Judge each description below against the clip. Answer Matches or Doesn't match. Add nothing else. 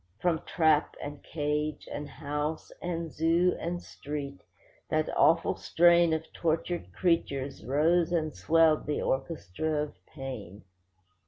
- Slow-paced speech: Matches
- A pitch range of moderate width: Doesn't match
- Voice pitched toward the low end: Doesn't match